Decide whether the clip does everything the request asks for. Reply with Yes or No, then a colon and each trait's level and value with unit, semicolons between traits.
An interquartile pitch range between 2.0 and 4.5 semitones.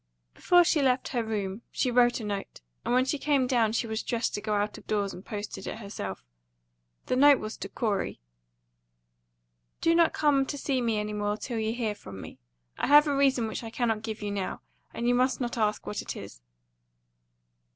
Yes: average, 3.7 semitones